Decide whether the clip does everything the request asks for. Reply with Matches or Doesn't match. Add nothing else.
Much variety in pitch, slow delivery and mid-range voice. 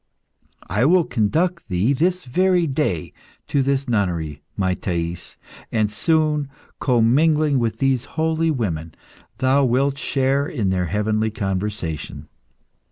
Doesn't match